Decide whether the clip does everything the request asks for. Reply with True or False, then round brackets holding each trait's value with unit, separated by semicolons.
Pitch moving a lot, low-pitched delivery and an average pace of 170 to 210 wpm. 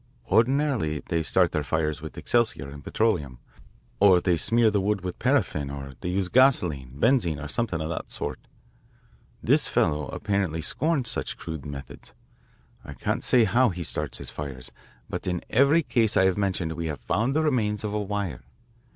True (6.8 semitones; 95 Hz; 175 wpm)